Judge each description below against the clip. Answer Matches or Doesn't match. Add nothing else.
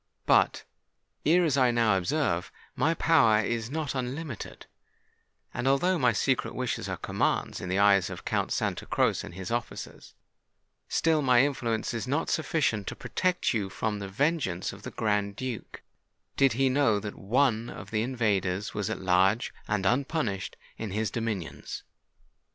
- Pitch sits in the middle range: Doesn't match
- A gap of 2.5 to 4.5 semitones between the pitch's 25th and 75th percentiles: Doesn't match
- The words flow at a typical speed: Matches